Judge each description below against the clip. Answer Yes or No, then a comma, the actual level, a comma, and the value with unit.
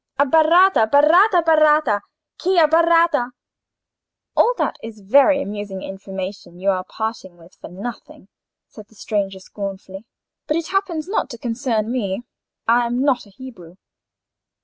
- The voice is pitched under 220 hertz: No, high, 235 Hz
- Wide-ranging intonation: Yes, wide, 7.7 semitones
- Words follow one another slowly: Yes, slow, 130 wpm